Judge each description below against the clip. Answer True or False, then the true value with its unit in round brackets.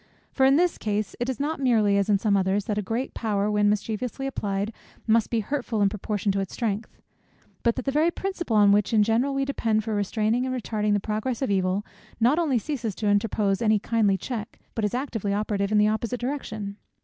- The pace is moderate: False (220 wpm)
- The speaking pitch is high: True (215 Hz)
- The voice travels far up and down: False (3.3 semitones)